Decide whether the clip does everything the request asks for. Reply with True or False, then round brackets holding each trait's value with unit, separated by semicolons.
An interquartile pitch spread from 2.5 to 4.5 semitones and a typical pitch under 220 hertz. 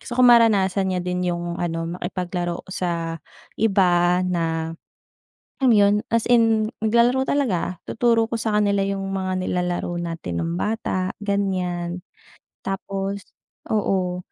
True (3.2 semitones; 190 Hz)